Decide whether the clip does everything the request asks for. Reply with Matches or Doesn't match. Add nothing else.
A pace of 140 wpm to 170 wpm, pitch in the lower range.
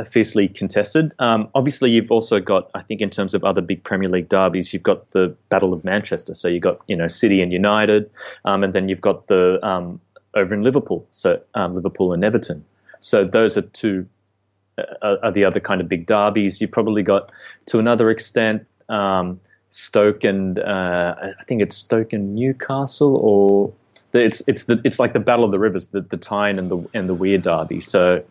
Doesn't match